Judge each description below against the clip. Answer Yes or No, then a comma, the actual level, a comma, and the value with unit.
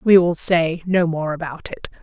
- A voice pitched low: No, medium, 165 Hz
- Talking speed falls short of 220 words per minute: Yes, fast, 205 wpm